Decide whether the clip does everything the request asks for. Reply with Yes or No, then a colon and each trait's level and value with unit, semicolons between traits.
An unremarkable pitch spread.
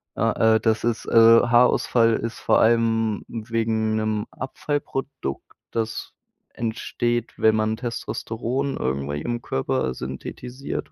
No: narrow, 1.6 semitones